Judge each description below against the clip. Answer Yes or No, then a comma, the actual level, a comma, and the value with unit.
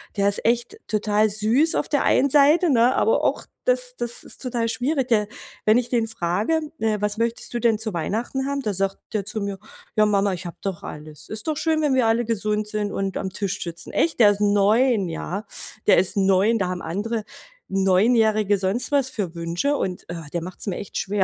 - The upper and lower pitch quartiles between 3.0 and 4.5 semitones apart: Yes, average, 3.7 semitones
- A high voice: Yes, high, 215 Hz